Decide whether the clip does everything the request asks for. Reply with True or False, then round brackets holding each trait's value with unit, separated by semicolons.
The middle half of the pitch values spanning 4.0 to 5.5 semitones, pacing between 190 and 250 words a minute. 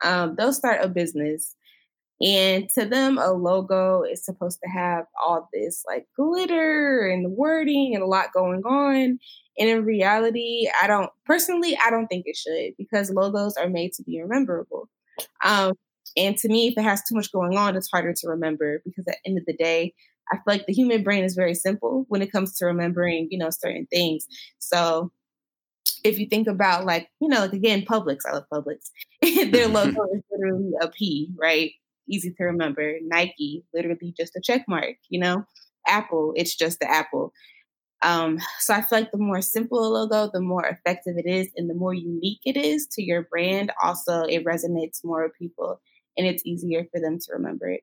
True (4.6 semitones; 200 wpm)